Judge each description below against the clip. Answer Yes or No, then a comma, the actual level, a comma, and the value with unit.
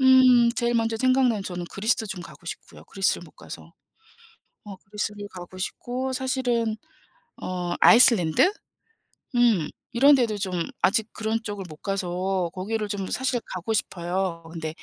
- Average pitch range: Yes, average, 4.6 semitones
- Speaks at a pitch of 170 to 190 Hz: No, high, 210 Hz